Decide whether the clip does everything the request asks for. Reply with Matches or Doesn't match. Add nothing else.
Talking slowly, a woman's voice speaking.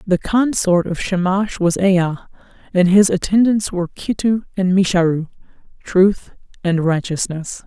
Matches